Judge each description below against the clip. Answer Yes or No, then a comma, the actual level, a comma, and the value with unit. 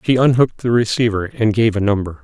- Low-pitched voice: Yes, low, 110 Hz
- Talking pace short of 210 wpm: No, fast, 215 wpm